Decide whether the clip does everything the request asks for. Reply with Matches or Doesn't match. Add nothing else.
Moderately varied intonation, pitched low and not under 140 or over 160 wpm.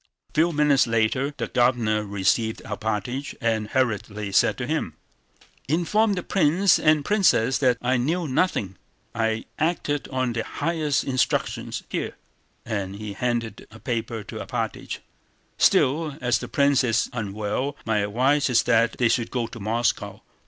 Matches